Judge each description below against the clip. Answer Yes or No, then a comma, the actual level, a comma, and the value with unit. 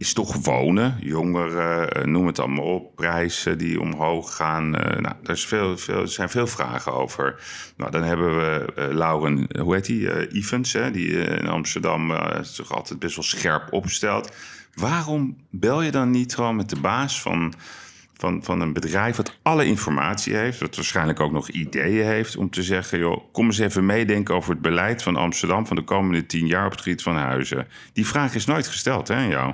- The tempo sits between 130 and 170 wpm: No, average, 195 wpm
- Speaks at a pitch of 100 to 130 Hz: No, very low, 90 Hz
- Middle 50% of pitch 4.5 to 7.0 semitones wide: Yes, average, 5.2 semitones